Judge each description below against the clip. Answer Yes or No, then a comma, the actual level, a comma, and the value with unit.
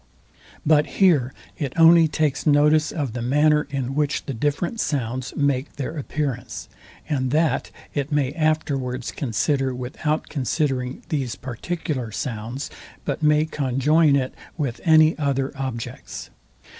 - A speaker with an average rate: No, slow, 130 wpm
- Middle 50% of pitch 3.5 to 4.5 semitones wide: No, average, 3.0 semitones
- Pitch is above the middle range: No, medium, 140 Hz